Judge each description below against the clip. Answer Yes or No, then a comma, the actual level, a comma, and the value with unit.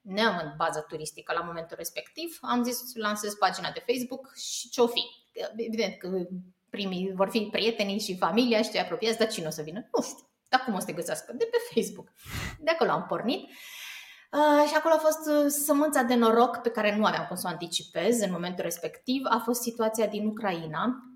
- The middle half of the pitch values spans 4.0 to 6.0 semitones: Yes, average, 4.8 semitones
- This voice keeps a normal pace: No, fast, 205 wpm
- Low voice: No, high, 225 Hz